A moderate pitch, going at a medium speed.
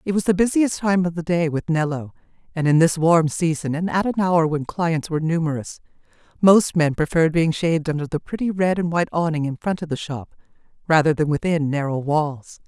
No: medium, 165 Hz; fast, 215 wpm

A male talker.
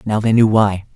Yes: male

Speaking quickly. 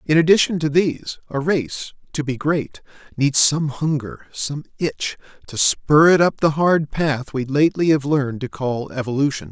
No: average, 175 wpm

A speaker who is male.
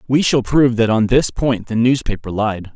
Yes: male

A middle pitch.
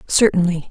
Yes: medium, 180 Hz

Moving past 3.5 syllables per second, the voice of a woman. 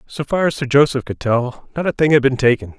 No: 5.8 syllables/s; male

